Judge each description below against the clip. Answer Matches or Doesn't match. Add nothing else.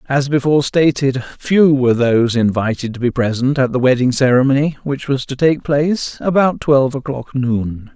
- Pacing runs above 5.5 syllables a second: Doesn't match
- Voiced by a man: Matches